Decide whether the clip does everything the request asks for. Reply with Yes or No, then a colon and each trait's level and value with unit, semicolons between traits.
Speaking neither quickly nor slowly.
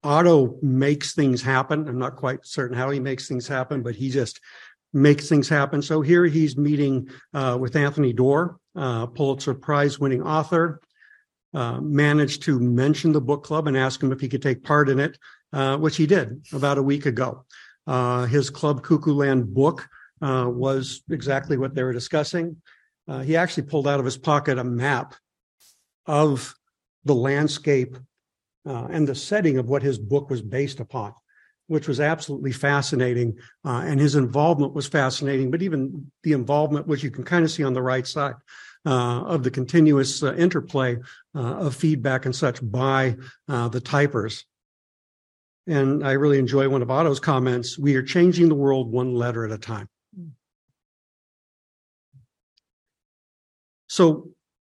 Yes: average, 165 wpm